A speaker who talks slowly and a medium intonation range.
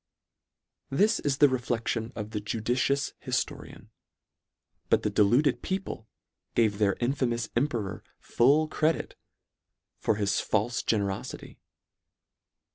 Yes: slow, 110 wpm; average, 4.5 semitones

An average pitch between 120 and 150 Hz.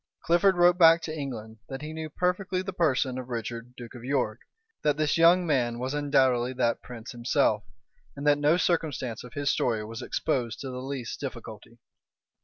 Yes: low, 135 Hz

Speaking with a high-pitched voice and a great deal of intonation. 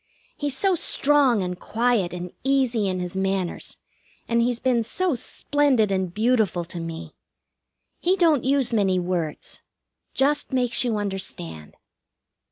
Yes: high, 225 Hz; wide, 6.4 semitones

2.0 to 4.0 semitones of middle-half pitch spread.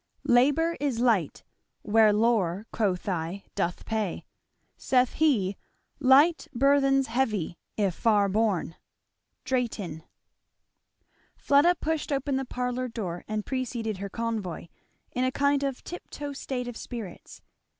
No: average, 5.1 semitones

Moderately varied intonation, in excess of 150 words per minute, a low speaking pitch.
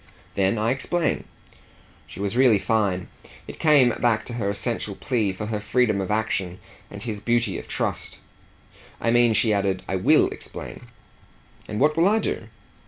Yes: average, 3.3 semitones; average, 170 wpm; low, 110 Hz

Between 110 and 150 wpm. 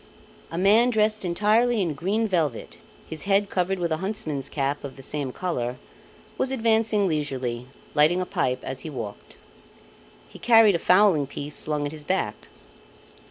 No: average, 160 wpm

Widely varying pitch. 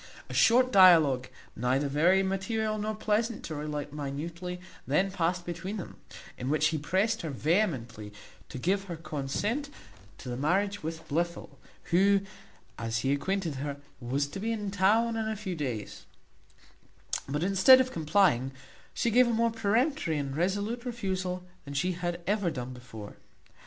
Yes: wide, 6.1 semitones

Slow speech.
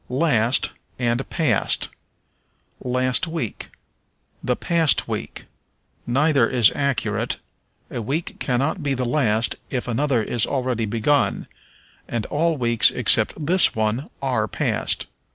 Yes: slow, 115 wpm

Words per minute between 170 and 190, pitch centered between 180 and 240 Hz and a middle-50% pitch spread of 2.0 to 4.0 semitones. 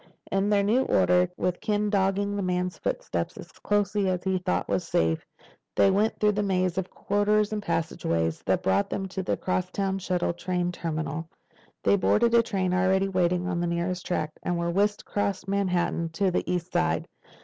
Yes: average, 185 wpm; medium, 185 Hz; narrow, 2.4 semitones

